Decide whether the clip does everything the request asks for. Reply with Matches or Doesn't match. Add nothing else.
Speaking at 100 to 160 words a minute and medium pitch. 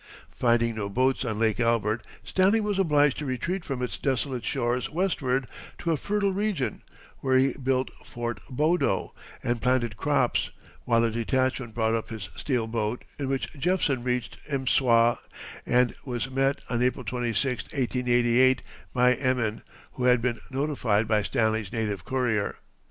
Doesn't match